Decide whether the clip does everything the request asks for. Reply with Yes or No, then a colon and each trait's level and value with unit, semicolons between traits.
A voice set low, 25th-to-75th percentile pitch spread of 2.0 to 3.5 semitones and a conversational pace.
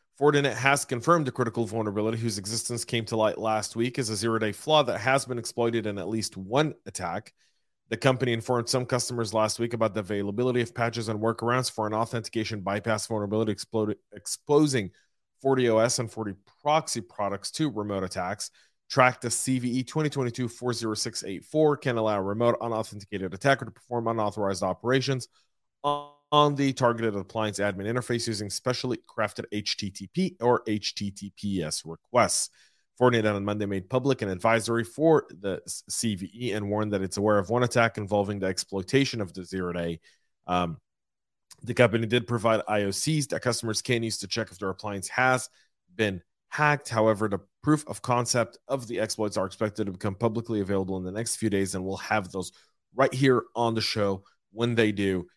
Yes: low, 115 Hz; average, 3.2 semitones; average, 170 wpm